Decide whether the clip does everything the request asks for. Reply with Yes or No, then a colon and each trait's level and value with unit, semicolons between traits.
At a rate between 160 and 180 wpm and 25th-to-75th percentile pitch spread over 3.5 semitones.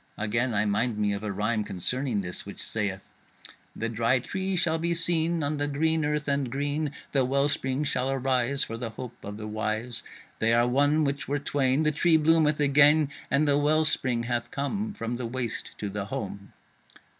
No: average, 195 wpm; average, 4.6 semitones